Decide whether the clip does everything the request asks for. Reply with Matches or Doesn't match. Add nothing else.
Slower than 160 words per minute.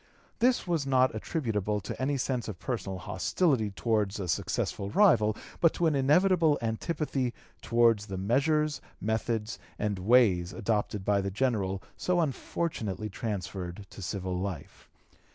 Matches